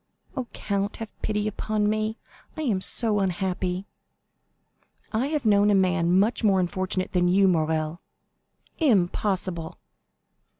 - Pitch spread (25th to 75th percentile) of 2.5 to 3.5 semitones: Yes, average, 3.0 semitones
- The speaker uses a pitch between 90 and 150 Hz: No, high, 195 Hz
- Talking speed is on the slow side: Yes, slow, 125 wpm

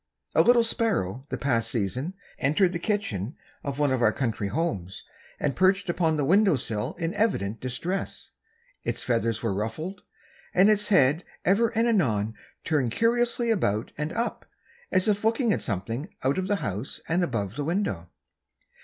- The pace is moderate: Yes, average, 165 wpm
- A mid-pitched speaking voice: Yes, medium, 155 Hz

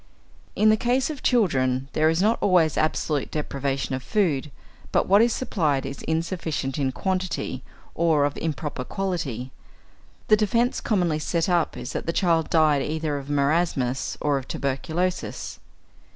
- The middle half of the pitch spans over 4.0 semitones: Yes, average, 4.9 semitones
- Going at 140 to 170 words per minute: Yes, average, 150 wpm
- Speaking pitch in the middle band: Yes, medium, 160 Hz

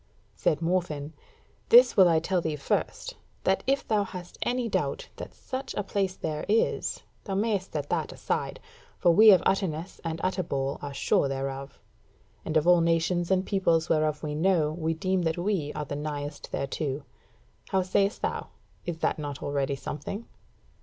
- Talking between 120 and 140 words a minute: No, average, 170 wpm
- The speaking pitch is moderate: Yes, medium, 165 Hz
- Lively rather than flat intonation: No, average, 4.3 semitones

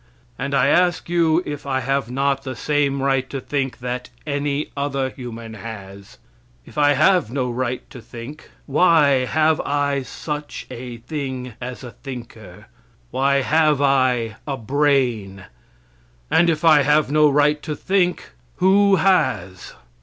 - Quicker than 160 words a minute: No, average, 145 wpm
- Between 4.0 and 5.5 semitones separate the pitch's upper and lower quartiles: No, average, 3.1 semitones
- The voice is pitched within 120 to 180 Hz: Yes, medium, 140 Hz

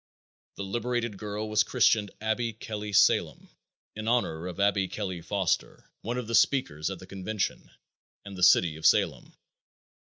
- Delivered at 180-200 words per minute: No, average, 155 wpm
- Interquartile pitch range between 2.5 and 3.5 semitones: Yes, average, 2.9 semitones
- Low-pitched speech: Yes, low, 105 Hz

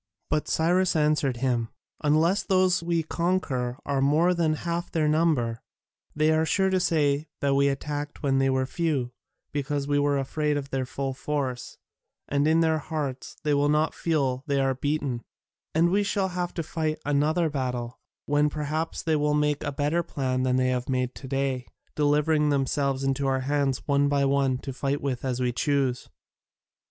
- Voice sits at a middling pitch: Yes, medium, 145 Hz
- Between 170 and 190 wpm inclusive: Yes, average, 185 wpm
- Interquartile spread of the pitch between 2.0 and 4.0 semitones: Yes, average, 2.8 semitones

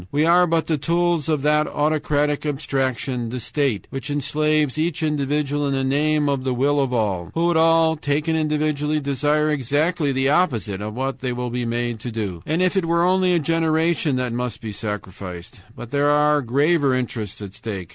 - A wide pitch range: No, average, 3.8 semitones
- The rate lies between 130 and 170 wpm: No, average, 195 wpm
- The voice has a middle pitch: Yes, medium, 145 Hz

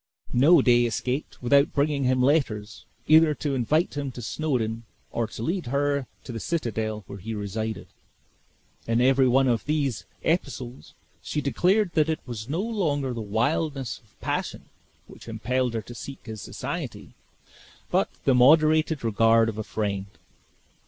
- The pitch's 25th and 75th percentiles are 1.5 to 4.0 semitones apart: No, average, 4.7 semitones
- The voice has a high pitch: No, low, 130 Hz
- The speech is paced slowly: No, average, 155 wpm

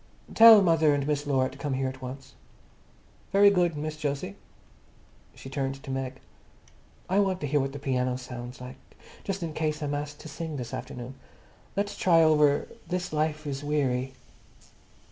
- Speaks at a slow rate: No, average, 170 wpm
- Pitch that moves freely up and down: No, average, 3.1 semitones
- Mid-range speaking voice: Yes, medium, 145 Hz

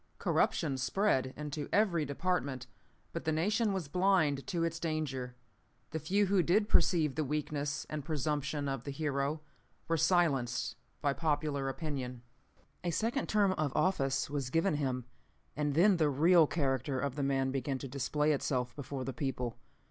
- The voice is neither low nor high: Yes, medium, 150 Hz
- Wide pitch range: No, average, 3.5 semitones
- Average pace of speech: Yes, average, 160 wpm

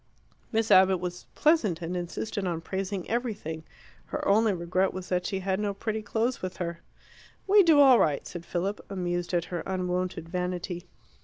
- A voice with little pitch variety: No, average, 3.0 semitones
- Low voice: No, medium, 185 Hz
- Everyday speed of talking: Yes, average, 170 wpm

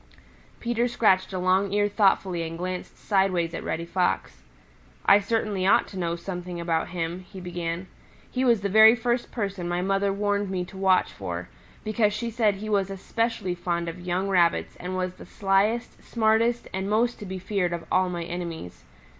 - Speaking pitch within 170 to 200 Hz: Yes, high, 190 Hz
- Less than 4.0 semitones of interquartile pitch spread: Yes, average, 2.9 semitones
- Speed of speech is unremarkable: Yes, average, 185 wpm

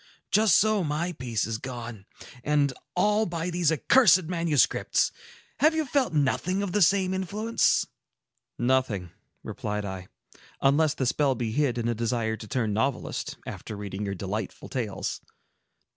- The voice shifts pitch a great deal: Yes, wide, 8.5 semitones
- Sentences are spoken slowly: No, average, 145 wpm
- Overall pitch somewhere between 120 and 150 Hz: Yes, medium, 140 Hz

